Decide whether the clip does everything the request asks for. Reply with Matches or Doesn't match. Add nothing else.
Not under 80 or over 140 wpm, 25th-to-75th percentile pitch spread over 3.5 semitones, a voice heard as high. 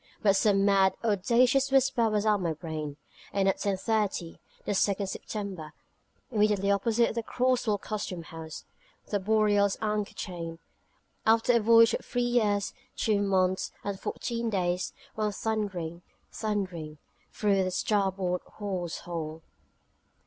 Doesn't match